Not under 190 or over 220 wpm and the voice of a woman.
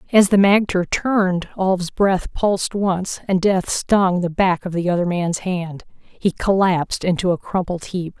No: average, 175 wpm; female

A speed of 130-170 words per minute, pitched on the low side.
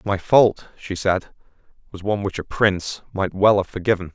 No: average, 190 wpm; very low, 95 Hz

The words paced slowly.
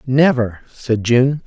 Yes: slow, 125 wpm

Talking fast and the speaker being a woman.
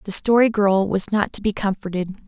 Yes: fast, 210 wpm; female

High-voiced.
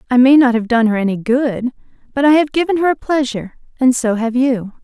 Yes: very high, 255 Hz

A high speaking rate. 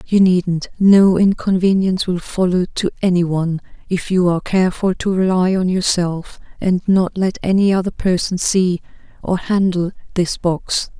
No: average, 155 wpm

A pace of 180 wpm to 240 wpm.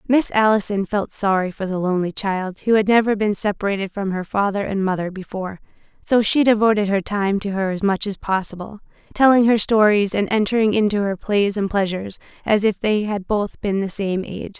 Yes: average, 200 wpm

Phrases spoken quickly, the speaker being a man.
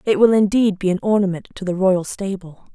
No: fast, 220 wpm; female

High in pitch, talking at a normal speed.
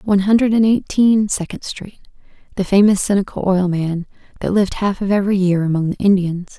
Yes: high, 195 Hz; average, 175 wpm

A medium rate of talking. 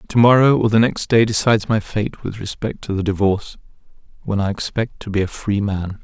No: fast, 220 wpm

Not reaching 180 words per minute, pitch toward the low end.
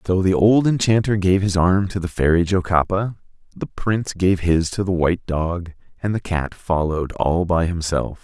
No: average, 190 wpm; very low, 90 Hz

